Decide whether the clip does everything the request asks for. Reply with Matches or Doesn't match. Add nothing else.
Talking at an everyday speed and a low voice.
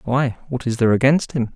Doesn't match